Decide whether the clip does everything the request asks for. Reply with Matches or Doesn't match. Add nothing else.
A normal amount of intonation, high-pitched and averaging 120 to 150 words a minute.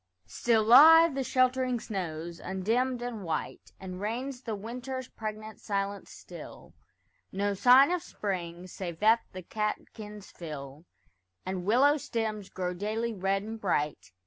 Matches